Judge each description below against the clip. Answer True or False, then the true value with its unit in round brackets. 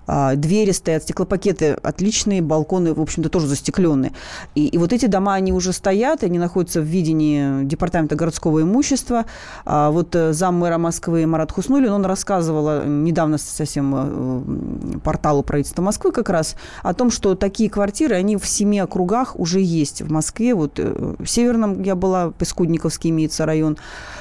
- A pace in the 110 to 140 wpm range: False (150 wpm)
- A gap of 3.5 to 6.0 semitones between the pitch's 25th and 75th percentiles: True (4.0 semitones)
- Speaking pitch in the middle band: True (170 Hz)